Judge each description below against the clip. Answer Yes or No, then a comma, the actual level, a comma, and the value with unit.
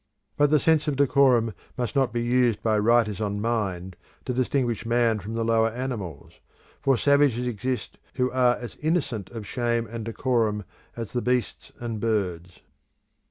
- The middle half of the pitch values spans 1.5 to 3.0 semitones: Yes, narrow, 2.6 semitones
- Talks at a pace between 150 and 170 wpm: Yes, average, 160 wpm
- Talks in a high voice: No, low, 120 Hz